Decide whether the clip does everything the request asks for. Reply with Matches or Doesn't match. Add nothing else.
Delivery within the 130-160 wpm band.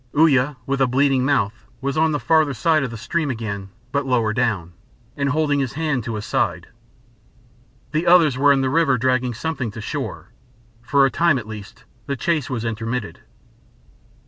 Doesn't match